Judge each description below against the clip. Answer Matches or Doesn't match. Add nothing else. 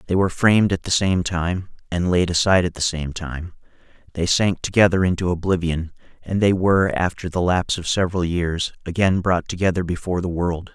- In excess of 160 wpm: Matches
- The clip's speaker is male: Matches